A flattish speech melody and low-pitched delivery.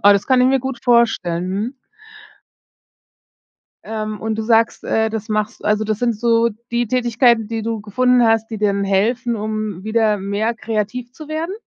No: narrow, 2.1 semitones; high, 225 Hz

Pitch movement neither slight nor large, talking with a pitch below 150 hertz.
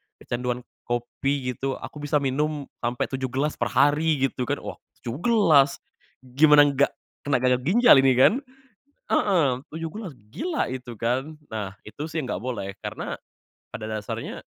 Yes: average, 3.5 semitones; low, 135 Hz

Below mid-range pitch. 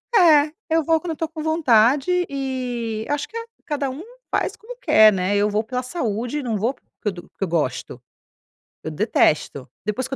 No: very high, 255 Hz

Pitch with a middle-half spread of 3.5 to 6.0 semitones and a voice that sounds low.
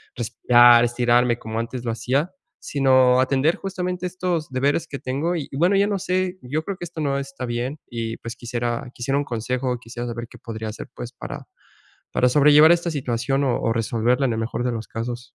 Yes: average, 4.0 semitones; low, 125 Hz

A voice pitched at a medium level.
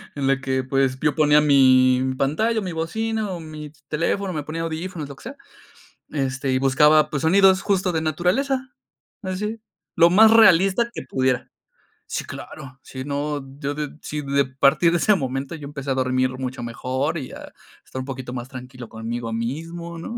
Yes: medium, 145 Hz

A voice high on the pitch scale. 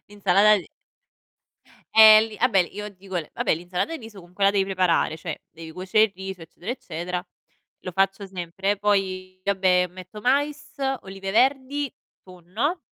Yes: high, 195 Hz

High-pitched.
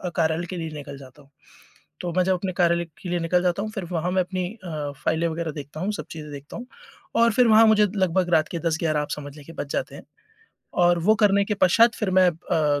No: medium, 175 Hz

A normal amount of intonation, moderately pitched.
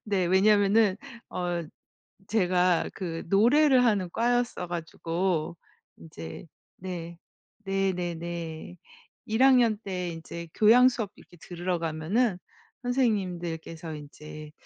Yes: average, 4.2 semitones; medium, 180 Hz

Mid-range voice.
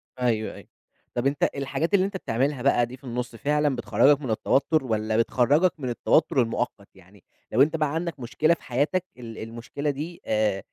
No: low, 130 Hz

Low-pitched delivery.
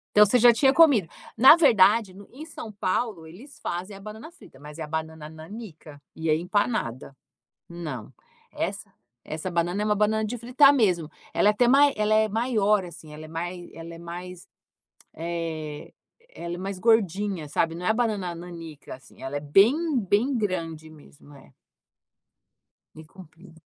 No: medium, 185 Hz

